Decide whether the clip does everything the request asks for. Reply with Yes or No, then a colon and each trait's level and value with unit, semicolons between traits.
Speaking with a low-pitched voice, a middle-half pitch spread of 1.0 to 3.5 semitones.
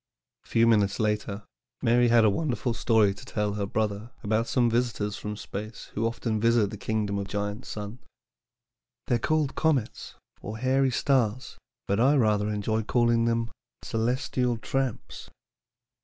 Yes: low, 115 Hz; narrow, 2.5 semitones